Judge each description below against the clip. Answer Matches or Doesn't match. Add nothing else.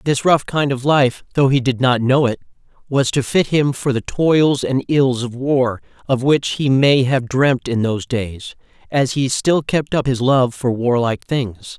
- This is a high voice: Doesn't match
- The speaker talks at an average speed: Doesn't match